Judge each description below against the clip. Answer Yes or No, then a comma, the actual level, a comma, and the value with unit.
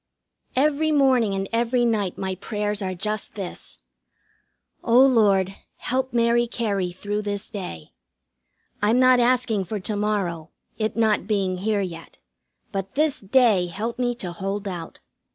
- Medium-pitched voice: No, high, 210 Hz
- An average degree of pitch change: Yes, average, 3.7 semitones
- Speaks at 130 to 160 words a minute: Yes, average, 145 wpm